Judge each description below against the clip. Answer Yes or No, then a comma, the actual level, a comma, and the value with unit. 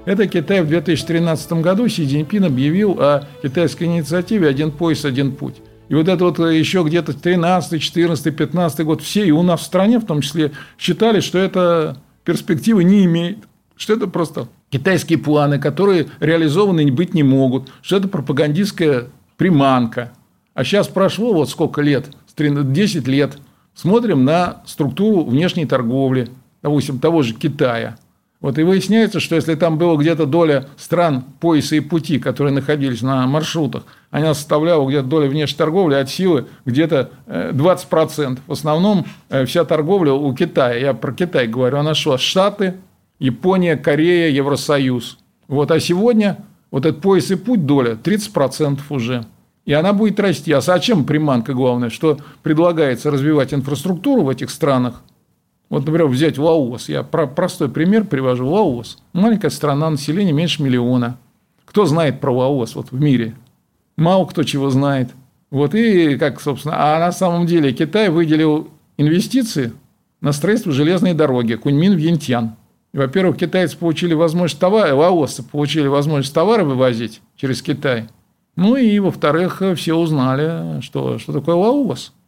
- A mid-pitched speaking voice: Yes, medium, 155 Hz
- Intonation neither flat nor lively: Yes, average, 4.3 semitones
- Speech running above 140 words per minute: Yes, average, 150 wpm